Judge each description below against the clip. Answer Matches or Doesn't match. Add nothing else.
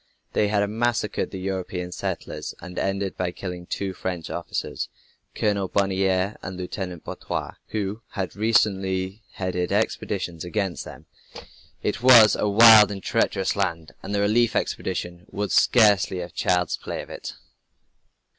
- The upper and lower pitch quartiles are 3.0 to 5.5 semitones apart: Doesn't match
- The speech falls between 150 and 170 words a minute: Doesn't match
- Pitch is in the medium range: Doesn't match